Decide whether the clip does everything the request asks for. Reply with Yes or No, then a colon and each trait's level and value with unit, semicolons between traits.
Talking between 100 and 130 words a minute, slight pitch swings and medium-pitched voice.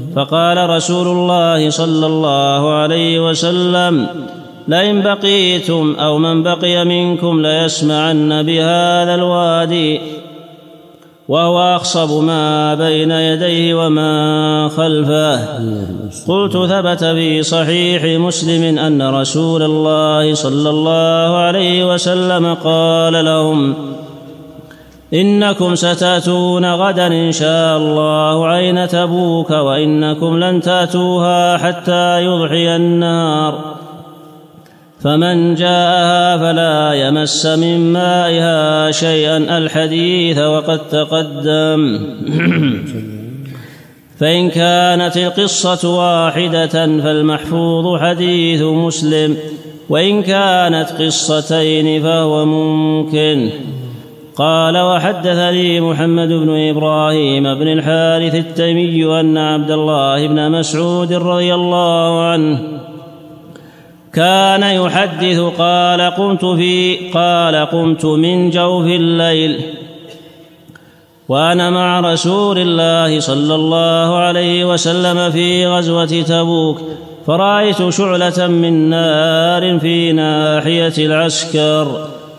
No: average, 85 wpm; narrow, 2.1 semitones; medium, 165 Hz